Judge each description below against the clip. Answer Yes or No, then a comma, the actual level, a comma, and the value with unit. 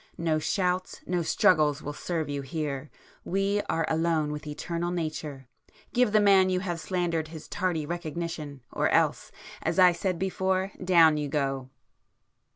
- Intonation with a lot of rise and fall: No, average, 3.4 semitones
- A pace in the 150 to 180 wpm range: No, average, 140 wpm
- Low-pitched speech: No, medium, 165 Hz